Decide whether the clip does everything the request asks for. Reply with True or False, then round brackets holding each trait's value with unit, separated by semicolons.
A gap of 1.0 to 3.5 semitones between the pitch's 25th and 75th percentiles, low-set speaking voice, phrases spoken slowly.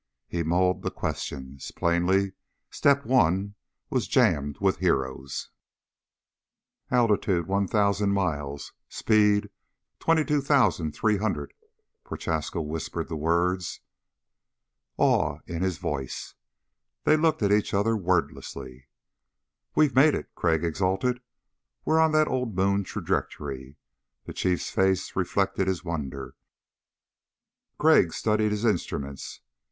False (5.0 semitones; 95 Hz; 105 wpm)